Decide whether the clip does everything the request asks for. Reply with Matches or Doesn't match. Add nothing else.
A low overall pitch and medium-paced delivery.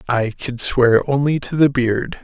Matches